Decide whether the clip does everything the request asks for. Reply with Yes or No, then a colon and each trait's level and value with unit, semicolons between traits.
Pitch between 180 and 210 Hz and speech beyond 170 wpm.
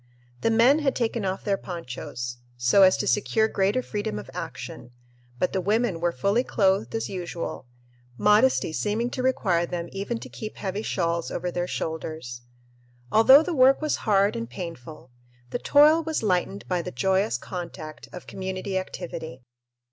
No: high, 190 Hz; average, 165 wpm